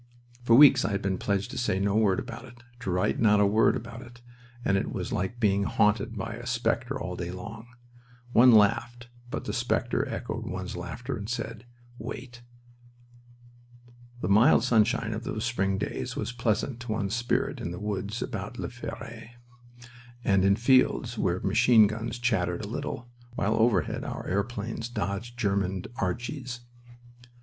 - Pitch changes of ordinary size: Yes, average, 3.4 semitones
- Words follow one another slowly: No, average, 165 wpm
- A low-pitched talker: Yes, low, 110 Hz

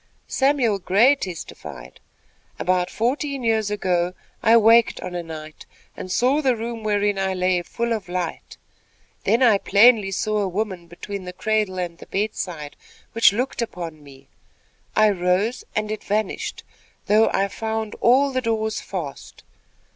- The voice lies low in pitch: No, high, 205 Hz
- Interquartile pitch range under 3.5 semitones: No, average, 3.9 semitones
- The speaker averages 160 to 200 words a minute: No, average, 150 wpm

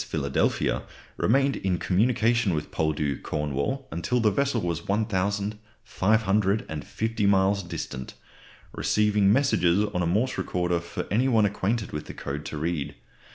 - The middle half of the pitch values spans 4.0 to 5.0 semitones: Yes, average, 4.6 semitones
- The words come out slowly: Yes, slow, 130 wpm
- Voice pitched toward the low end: Yes, low, 100 Hz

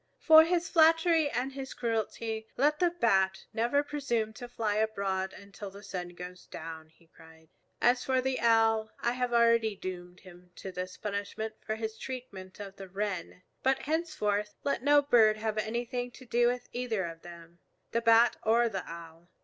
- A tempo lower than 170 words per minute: No, average, 175 wpm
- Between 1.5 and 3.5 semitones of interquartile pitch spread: No, average, 4.6 semitones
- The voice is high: Yes, high, 220 Hz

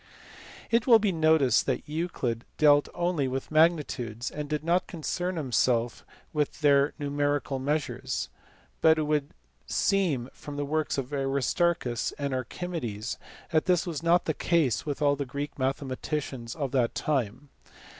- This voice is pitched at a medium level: Yes, medium, 145 Hz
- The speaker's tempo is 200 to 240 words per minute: No, average, 155 wpm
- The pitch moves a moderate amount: Yes, average, 3.3 semitones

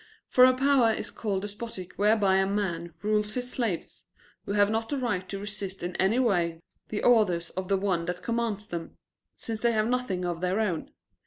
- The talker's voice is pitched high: Yes, high, 205 Hz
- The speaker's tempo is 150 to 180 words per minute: No, average, 195 wpm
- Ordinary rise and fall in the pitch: Yes, average, 3.6 semitones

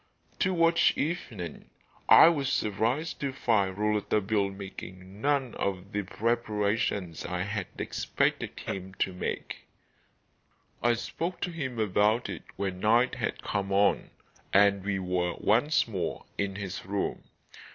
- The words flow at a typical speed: No, slow, 130 wpm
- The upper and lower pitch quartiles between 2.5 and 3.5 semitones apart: No, average, 3.9 semitones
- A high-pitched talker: No, low, 105 Hz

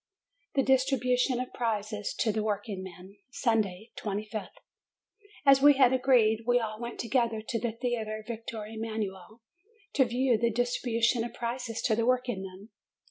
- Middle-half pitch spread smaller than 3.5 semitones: Yes, narrow, 2.4 semitones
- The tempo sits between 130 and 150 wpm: Yes, average, 140 wpm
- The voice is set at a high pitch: Yes, high, 230 Hz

